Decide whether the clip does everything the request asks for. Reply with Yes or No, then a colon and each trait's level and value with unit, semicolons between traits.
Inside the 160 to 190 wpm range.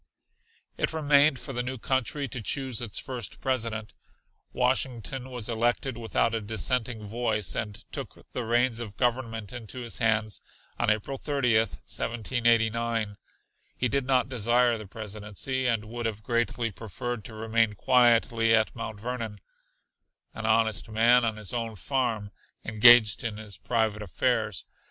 No: average, 145 wpm